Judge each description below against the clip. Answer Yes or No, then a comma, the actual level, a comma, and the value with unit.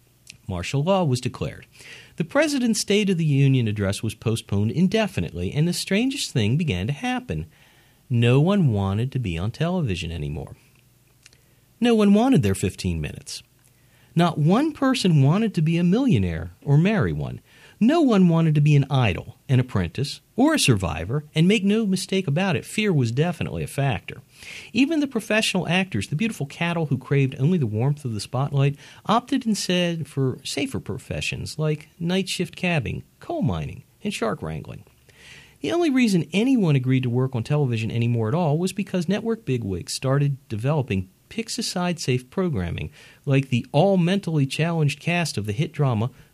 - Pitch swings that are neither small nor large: No, wide, 7.0 semitones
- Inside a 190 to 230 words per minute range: No, average, 170 wpm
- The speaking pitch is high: No, medium, 145 Hz